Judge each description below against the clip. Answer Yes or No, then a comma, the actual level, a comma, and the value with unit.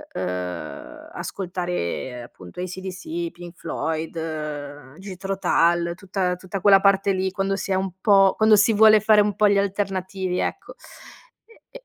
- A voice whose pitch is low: No, medium, 185 Hz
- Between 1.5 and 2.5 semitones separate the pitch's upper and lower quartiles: No, average, 2.9 semitones